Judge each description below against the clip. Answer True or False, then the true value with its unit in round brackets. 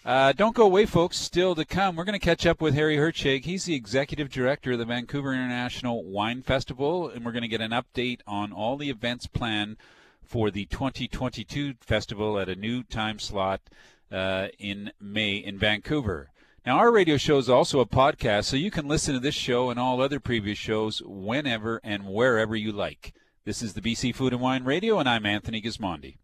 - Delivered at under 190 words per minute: False (205 wpm)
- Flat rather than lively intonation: False (4.6 semitones)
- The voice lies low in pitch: True (125 Hz)